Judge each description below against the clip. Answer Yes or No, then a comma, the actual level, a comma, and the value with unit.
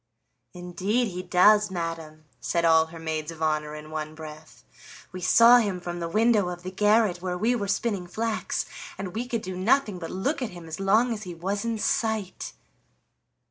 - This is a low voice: No, medium, 185 Hz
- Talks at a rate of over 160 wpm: Yes, average, 190 wpm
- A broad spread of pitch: No, average, 4.5 semitones